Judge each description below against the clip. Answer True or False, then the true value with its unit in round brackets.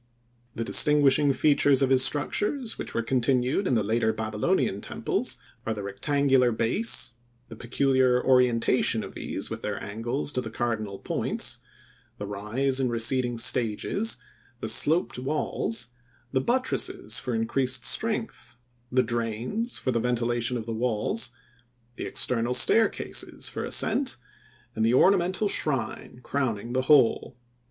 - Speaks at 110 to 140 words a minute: True (135 wpm)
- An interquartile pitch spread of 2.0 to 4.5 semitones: True (3.4 semitones)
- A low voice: True (125 Hz)